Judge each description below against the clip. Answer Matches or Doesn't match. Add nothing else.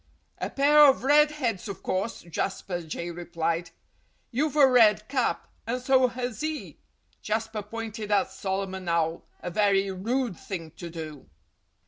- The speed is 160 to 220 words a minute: Doesn't match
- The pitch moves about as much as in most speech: Doesn't match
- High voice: Matches